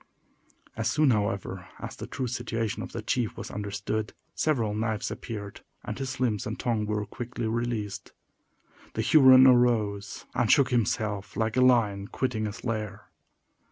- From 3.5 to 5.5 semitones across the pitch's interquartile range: No, average, 2.8 semitones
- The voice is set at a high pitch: No, low, 110 Hz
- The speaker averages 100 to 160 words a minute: Yes, average, 155 wpm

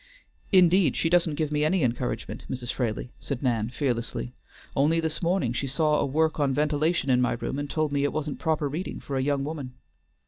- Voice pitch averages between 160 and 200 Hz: No, medium, 145 Hz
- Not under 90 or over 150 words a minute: No, fast, 205 wpm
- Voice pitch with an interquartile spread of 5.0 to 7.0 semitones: No, average, 3.7 semitones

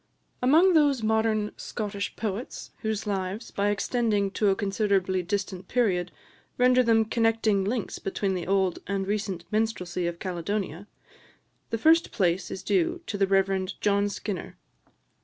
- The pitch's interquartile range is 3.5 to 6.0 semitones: No, average, 2.8 semitones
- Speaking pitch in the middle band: No, high, 205 Hz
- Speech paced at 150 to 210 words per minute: No, average, 140 wpm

